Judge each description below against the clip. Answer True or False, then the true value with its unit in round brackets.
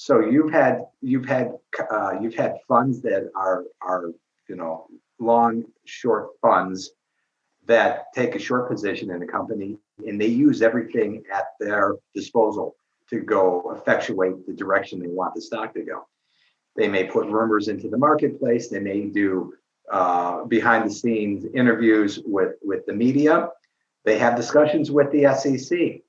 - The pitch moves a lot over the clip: False (4.7 semitones)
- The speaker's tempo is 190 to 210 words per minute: False (155 wpm)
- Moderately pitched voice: False (115 Hz)